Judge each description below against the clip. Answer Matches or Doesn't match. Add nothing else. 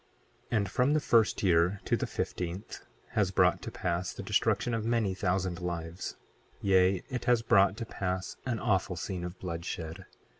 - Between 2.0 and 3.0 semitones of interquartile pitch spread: Doesn't match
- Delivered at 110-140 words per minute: Doesn't match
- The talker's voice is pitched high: Doesn't match